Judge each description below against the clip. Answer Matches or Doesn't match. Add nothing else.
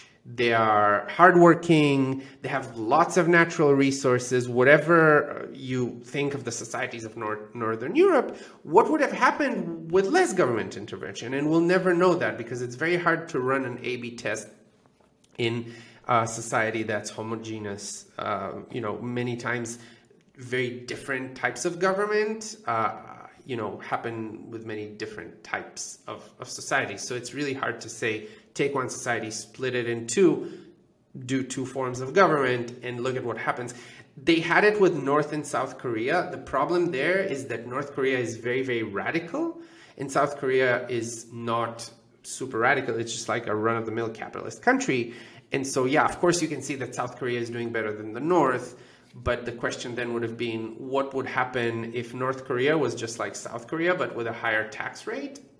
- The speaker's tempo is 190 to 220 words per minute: Doesn't match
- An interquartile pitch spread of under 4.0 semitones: Doesn't match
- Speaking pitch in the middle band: Doesn't match